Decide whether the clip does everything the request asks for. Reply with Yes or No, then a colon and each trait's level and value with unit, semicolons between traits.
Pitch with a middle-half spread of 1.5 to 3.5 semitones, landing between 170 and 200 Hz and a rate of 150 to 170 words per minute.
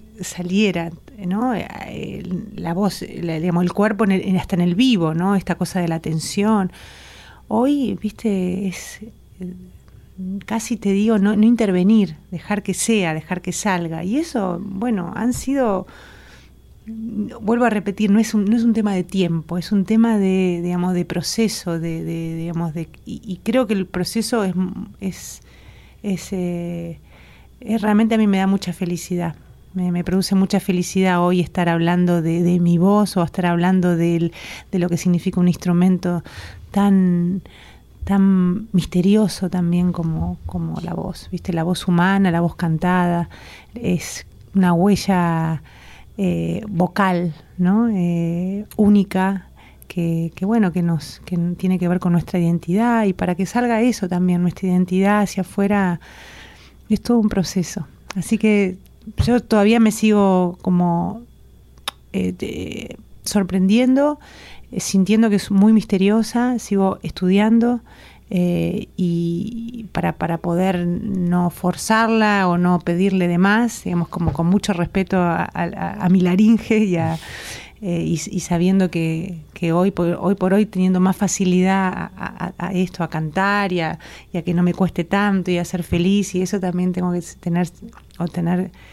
Yes: average, 2.8 semitones; medium, 185 Hz; average, 160 wpm